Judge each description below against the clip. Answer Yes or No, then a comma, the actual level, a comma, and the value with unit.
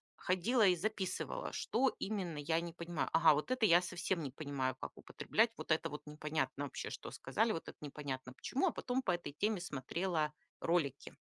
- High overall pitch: No, medium, 170 Hz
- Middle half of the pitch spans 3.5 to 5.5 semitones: Yes, average, 4.6 semitones